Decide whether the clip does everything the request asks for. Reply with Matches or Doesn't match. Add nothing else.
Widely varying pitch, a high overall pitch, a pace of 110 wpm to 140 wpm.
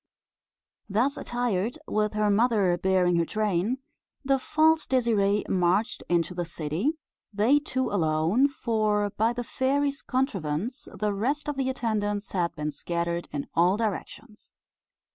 Matches